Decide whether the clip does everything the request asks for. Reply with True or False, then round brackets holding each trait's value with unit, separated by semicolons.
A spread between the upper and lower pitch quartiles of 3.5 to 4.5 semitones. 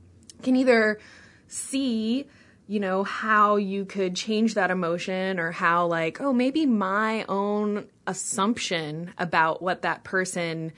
True (4.0 semitones)